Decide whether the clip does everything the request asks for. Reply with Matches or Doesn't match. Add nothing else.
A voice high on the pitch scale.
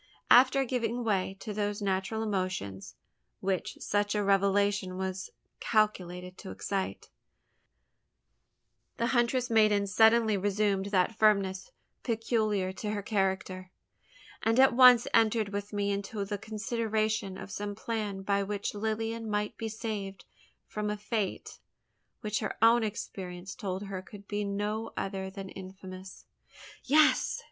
Matches